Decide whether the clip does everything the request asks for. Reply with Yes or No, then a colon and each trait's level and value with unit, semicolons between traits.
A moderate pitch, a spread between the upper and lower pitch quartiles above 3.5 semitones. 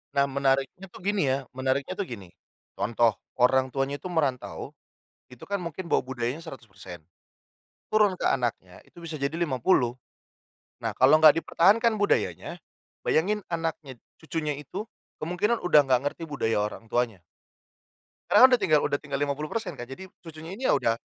Yes: medium, 145 Hz; average, 5.2 semitones